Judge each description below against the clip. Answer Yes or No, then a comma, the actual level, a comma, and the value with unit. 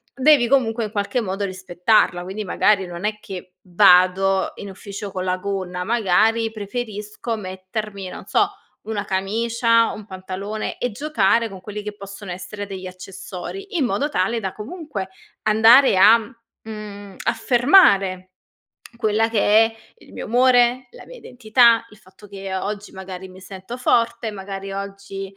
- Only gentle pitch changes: No, average, 3.2 semitones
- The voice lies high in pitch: Yes, high, 205 Hz